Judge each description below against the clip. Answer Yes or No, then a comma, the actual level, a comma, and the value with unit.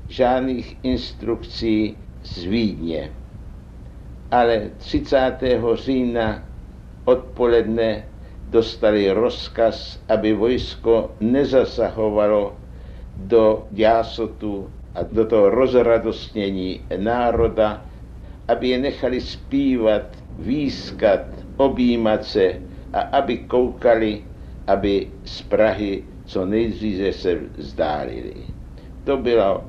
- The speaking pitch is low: Yes, low, 110 Hz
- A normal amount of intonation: Yes, average, 3.1 semitones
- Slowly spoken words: Yes, slow, 80 wpm